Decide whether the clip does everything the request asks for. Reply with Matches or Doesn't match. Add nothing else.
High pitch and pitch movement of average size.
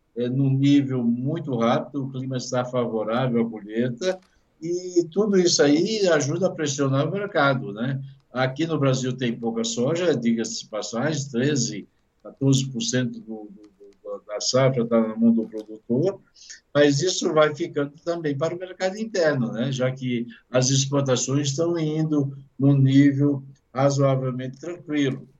Doesn't match